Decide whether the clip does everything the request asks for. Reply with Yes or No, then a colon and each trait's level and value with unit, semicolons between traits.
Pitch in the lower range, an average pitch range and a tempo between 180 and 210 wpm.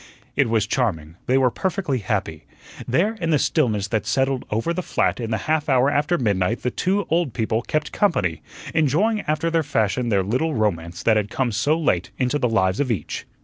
No: low, 125 Hz; wide, 6.5 semitones; average, 200 wpm